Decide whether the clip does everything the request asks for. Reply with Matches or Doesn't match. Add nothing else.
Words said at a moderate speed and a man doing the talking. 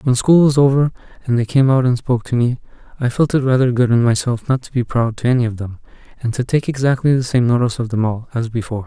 Doesn't match